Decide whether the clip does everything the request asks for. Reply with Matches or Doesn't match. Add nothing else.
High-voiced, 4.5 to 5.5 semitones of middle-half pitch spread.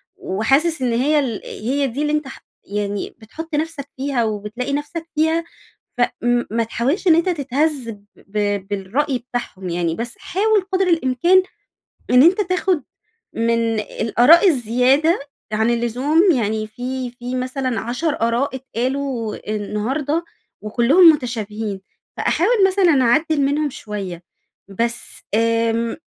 Matches